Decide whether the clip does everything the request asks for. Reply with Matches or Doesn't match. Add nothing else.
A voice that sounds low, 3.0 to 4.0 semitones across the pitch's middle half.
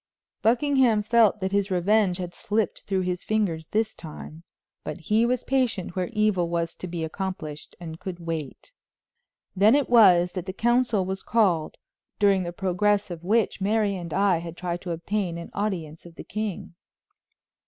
Doesn't match